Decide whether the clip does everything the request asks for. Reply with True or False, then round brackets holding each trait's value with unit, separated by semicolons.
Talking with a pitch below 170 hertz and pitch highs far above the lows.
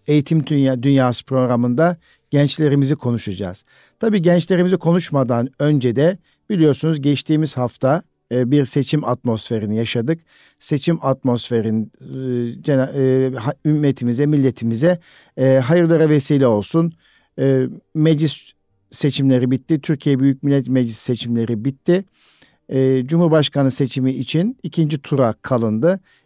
False (140 Hz; 3.9 semitones)